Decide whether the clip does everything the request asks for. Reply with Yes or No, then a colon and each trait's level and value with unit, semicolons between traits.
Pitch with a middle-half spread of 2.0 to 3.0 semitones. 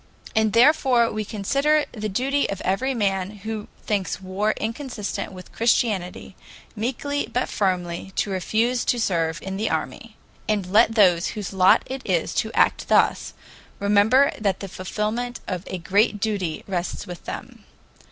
No: average, 3.7 semitones